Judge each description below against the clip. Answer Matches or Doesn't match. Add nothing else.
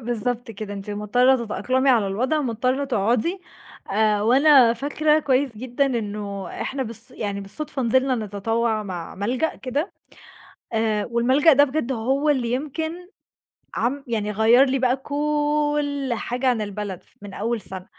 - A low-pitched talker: Doesn't match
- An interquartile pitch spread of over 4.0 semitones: Matches